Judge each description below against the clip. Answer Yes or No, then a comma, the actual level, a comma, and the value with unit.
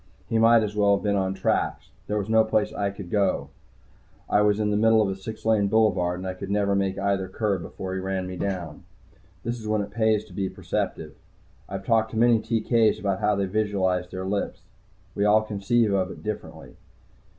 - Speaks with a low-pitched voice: Yes, low, 100 Hz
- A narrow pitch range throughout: Yes, narrow, 2.2 semitones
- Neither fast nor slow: No, fast, 210 wpm